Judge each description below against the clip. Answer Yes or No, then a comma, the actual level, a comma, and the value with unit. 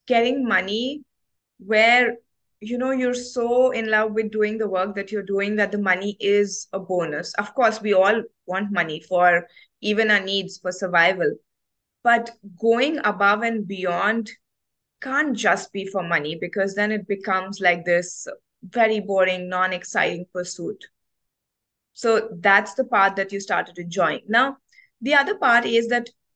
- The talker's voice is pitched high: Yes, high, 205 Hz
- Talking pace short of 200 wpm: Yes, average, 160 wpm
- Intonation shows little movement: No, average, 3.7 semitones